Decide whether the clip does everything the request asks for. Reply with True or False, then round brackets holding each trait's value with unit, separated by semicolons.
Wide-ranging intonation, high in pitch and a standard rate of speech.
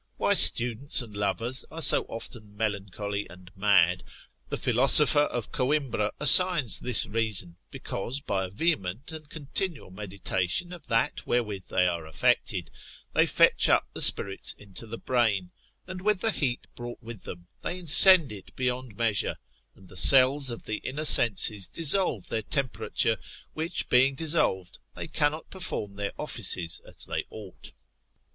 False (6.6 semitones; 115 Hz; 150 wpm)